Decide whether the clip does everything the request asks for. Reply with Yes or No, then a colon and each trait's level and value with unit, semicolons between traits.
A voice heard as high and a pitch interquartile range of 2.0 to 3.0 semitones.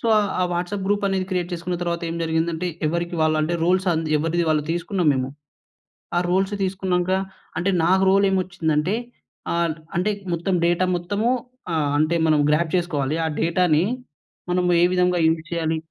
No: medium, 175 Hz; narrow, 2.5 semitones